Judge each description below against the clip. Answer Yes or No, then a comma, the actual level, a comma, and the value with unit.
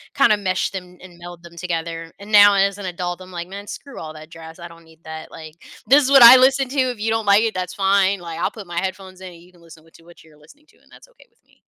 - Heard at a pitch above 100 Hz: Yes, medium, 185 Hz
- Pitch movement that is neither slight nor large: Yes, average, 3.4 semitones